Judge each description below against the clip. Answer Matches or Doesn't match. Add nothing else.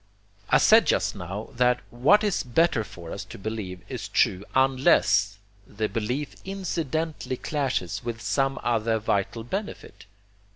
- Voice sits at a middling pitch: Doesn't match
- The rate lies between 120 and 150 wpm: Matches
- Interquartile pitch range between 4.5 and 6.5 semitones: Matches